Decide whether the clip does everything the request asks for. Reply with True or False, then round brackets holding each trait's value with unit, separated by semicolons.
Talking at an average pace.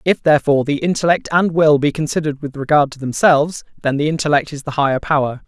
False (210 wpm)